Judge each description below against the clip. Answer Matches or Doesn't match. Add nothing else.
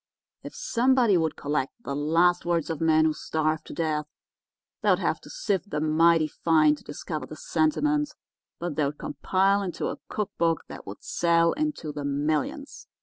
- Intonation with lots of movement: Doesn't match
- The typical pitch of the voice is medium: Matches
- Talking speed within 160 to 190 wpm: Matches